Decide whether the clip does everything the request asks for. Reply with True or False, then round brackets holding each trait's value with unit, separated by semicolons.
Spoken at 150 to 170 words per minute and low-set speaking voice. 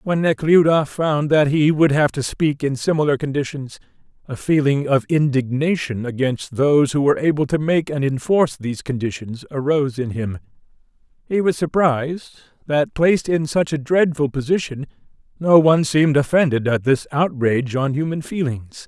False (160 wpm; 145 Hz)